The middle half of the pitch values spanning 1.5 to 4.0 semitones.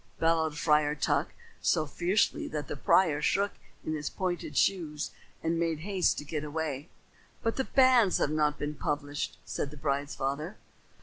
Yes: average, 3.0 semitones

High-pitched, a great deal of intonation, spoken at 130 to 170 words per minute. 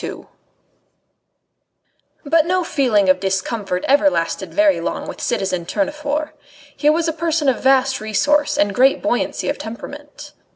Yes: very high, 275 Hz; wide, 6.5 semitones; average, 140 wpm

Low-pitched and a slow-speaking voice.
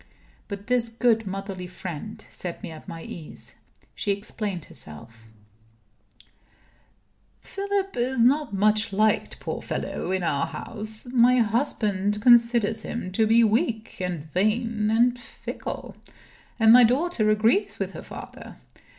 No: high, 215 Hz; slow, 130 wpm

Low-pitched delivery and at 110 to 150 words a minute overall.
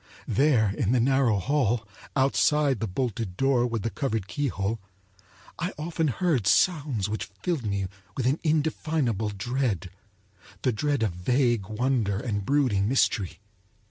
Yes: low, 120 Hz; slow, 135 wpm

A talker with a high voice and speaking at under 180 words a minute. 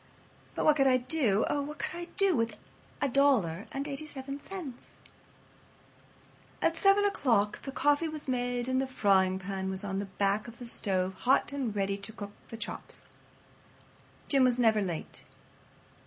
Yes: high, 245 Hz; average, 170 wpm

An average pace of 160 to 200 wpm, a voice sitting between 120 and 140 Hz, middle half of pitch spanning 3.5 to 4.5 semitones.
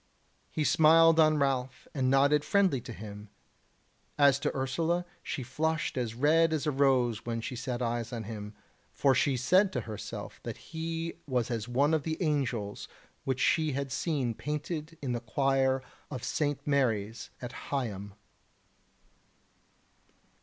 No: average, 150 wpm; low, 135 Hz; average, 4.2 semitones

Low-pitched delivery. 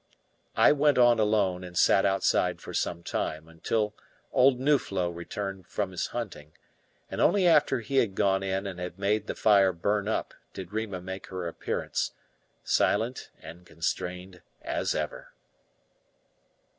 Yes: very low, 95 Hz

